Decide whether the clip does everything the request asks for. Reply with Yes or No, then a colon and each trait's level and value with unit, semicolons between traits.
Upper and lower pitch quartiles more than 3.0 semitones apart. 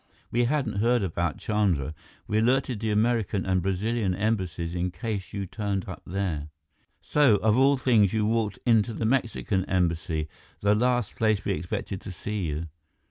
Yes: average, 3.7 semitones